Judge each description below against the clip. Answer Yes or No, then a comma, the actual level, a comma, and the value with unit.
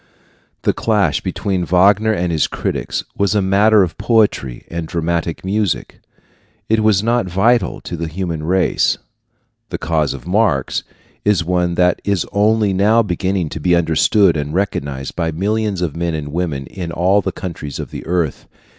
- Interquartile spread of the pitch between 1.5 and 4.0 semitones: Yes, average, 3.6 semitones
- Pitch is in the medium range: No, very low, 90 Hz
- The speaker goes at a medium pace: Yes, average, 165 wpm